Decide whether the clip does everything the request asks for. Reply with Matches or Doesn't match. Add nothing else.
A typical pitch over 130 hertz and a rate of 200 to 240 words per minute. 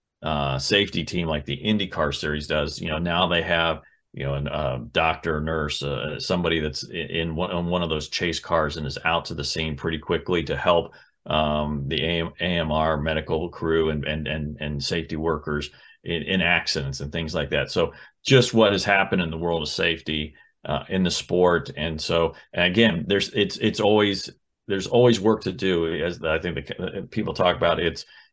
Doesn't match